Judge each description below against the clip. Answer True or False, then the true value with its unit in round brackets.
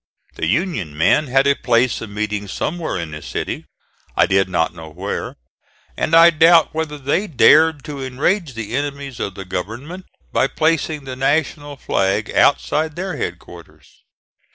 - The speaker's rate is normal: True (160 wpm)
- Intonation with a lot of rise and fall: True (7.6 semitones)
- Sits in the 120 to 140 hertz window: True (135 Hz)